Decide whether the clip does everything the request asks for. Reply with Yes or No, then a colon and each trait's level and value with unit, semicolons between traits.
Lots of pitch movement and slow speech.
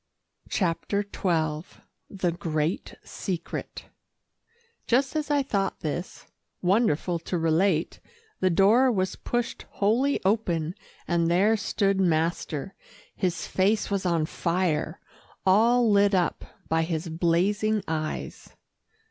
No: average, 3.8 semitones; slow, 110 wpm